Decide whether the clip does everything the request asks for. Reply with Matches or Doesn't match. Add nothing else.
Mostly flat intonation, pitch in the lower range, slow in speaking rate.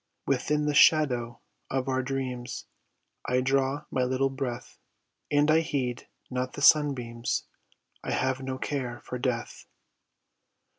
Matches